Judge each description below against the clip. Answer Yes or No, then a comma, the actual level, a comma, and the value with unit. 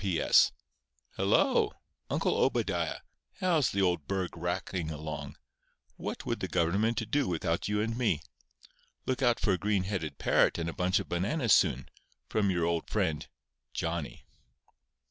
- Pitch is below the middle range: Yes, very low, 90 Hz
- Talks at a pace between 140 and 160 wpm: Yes, average, 145 wpm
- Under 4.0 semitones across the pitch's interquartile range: No, average, 4.3 semitones